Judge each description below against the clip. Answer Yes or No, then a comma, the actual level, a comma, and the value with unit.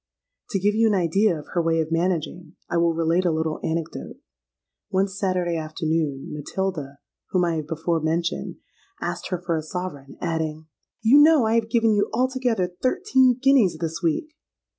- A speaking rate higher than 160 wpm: Yes, average, 170 wpm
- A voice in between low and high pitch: Yes, medium, 175 Hz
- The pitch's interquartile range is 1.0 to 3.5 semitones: No, average, 4.8 semitones